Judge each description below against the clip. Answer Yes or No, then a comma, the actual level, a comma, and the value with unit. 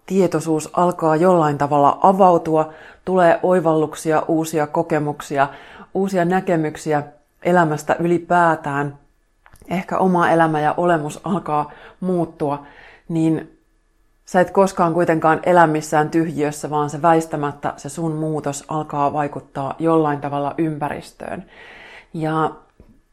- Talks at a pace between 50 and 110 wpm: Yes, average, 105 wpm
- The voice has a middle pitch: Yes, medium, 160 Hz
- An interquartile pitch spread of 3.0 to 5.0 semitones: No, narrow, 2.6 semitones